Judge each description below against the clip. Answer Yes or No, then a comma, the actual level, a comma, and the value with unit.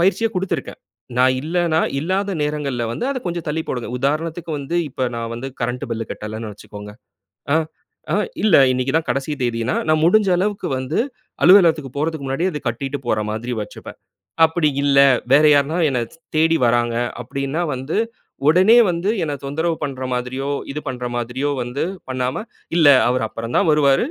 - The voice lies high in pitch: No, medium, 140 Hz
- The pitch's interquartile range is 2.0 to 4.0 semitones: No, average, 4.7 semitones